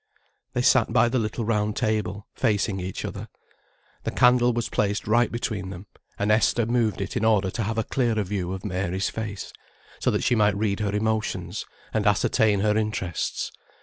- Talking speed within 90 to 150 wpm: No, average, 180 wpm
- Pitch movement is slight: Yes, narrow, 2.1 semitones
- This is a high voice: No, low, 105 Hz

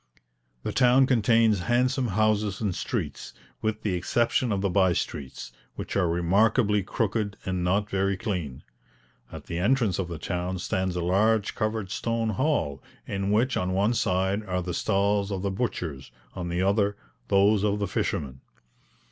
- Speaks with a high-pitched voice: No, low, 100 Hz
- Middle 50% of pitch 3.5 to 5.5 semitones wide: No, average, 3.1 semitones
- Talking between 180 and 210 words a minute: No, average, 165 wpm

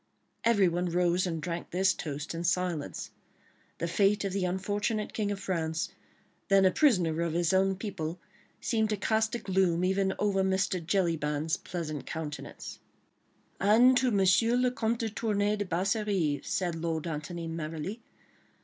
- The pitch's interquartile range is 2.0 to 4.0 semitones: Yes, average, 3.6 semitones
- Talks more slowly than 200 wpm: Yes, average, 150 wpm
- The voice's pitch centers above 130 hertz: Yes, medium, 185 Hz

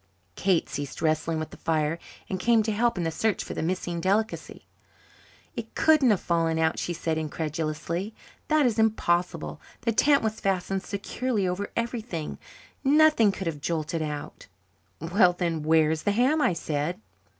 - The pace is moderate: Yes, average, 165 wpm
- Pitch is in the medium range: Yes, medium, 180 Hz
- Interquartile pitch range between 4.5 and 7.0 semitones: Yes, wide, 5.4 semitones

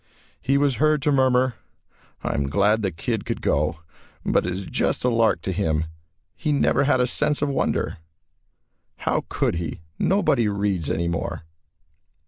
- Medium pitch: No, low, 110 Hz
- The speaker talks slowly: No, average, 160 wpm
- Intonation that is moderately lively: No, wide, 8.3 semitones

